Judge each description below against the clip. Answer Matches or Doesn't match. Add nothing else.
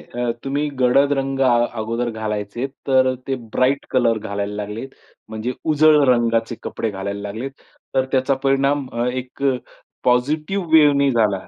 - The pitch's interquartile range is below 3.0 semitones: Doesn't match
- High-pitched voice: Doesn't match